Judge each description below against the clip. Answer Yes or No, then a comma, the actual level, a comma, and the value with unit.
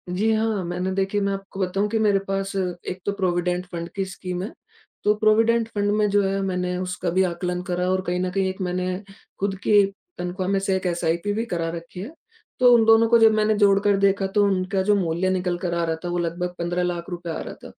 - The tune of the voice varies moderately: No, narrow, 2.3 semitones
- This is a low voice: No, high, 190 Hz